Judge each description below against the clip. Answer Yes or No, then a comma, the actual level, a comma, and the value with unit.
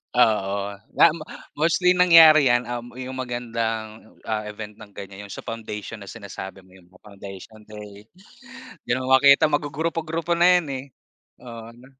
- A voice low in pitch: Yes, low, 120 Hz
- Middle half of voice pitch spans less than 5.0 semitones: No, wide, 5.4 semitones